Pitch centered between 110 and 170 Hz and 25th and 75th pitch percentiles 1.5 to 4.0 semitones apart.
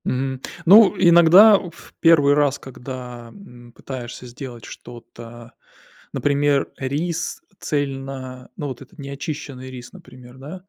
Yes: low, 135 Hz; average, 3.4 semitones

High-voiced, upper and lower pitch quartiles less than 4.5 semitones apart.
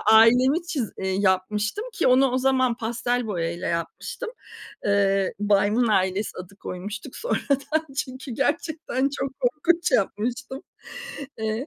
No: high, 240 Hz; average, 5.0 semitones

